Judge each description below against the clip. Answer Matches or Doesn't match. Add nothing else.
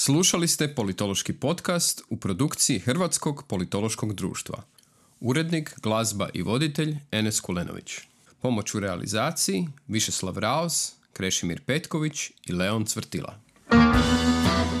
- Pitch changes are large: Matches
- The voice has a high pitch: Doesn't match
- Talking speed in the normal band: Doesn't match